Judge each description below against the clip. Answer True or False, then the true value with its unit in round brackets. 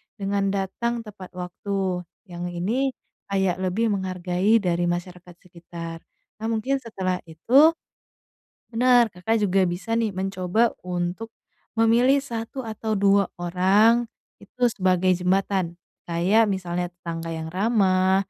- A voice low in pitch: False (190 Hz)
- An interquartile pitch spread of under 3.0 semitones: False (3.9 semitones)